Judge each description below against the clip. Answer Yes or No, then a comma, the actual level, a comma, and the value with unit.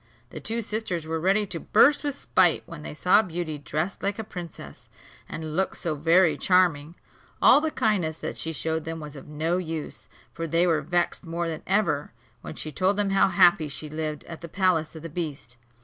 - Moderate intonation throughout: Yes, average, 3.2 semitones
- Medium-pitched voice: Yes, medium, 165 Hz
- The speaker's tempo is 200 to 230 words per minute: Yes, fast, 205 wpm